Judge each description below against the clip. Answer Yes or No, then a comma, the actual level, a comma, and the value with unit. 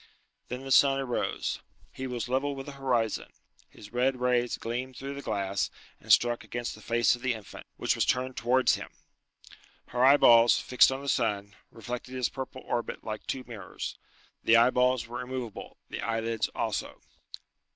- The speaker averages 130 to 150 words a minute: No, average, 170 wpm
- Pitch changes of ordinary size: No, narrow, 2.0 semitones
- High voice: No, low, 125 Hz